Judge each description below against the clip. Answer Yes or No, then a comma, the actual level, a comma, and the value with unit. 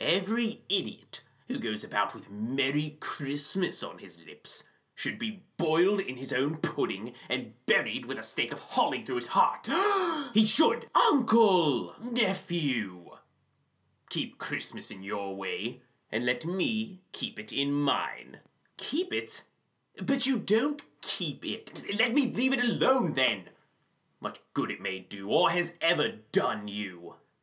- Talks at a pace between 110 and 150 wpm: Yes, average, 145 wpm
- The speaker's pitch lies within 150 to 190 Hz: Yes, medium, 185 Hz